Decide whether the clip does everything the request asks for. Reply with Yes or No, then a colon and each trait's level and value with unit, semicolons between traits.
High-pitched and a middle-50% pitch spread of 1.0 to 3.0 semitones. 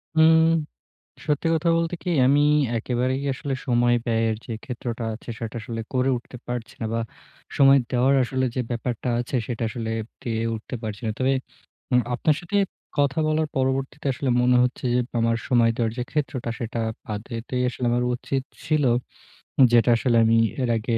No: low, 125 Hz; average, 2.7 semitones